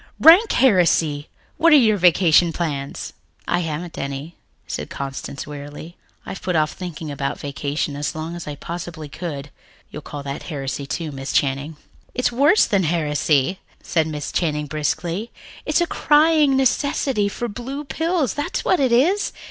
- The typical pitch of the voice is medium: Yes, medium, 165 Hz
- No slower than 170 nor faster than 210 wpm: No, average, 155 wpm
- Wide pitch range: Yes, wide, 8.5 semitones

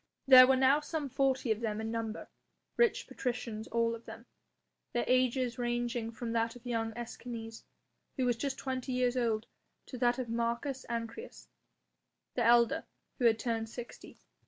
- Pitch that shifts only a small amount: Yes, narrow, 1.9 semitones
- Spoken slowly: No, average, 160 wpm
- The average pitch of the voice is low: No, high, 240 Hz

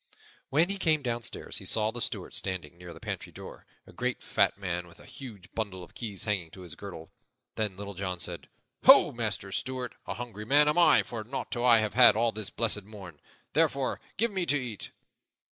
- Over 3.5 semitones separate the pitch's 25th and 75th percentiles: Yes, average, 5.0 semitones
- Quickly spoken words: Yes, fast, 210 wpm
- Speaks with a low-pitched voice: Yes, low, 110 Hz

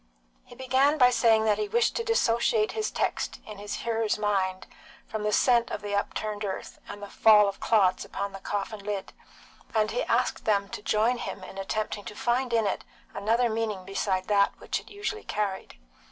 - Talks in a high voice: Yes, high, 215 Hz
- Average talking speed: Yes, average, 195 wpm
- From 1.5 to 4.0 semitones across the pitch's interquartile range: Yes, average, 2.8 semitones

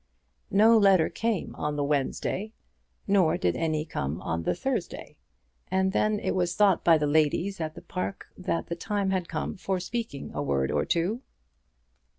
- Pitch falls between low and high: Yes, medium, 175 Hz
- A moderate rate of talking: Yes, average, 170 wpm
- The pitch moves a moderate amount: Yes, average, 4.8 semitones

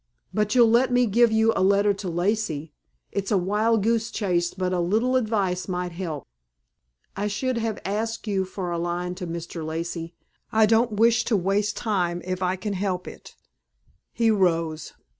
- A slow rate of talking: No, average, 180 wpm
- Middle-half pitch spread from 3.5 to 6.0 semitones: Yes, average, 3.8 semitones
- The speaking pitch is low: No, high, 200 Hz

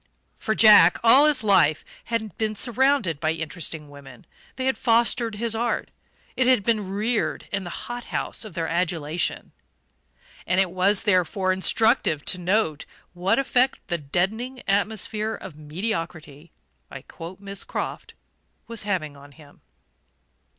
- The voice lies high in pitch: Yes, high, 195 Hz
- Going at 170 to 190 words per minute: No, average, 145 wpm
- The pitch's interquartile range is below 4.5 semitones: No, wide, 5.5 semitones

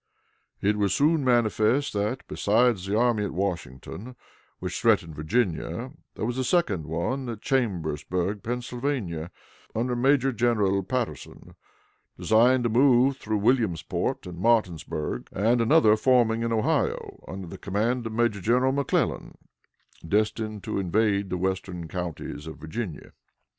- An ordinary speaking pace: No, slow, 130 wpm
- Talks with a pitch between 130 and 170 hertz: No, low, 110 Hz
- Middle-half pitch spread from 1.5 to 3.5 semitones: No, average, 4.7 semitones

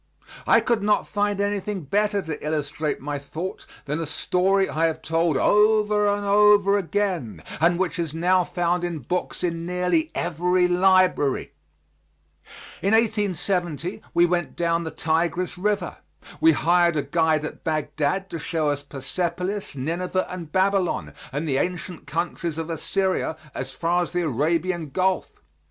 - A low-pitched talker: No, medium, 175 Hz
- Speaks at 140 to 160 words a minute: Yes, average, 150 wpm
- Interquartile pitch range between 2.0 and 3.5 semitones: Yes, average, 3.0 semitones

